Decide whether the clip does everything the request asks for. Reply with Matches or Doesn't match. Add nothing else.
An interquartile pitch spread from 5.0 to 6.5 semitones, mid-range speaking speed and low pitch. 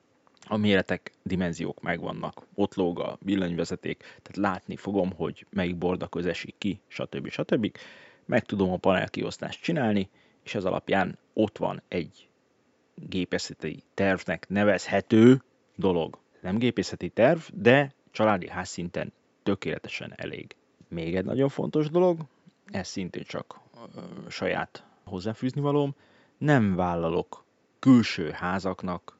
Matches